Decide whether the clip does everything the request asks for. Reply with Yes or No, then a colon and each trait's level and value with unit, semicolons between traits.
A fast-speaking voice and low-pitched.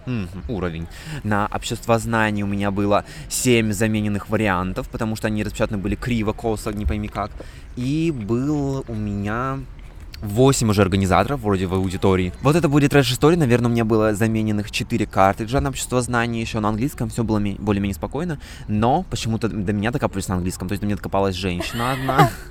Yes: fast, 180 wpm; low, 110 Hz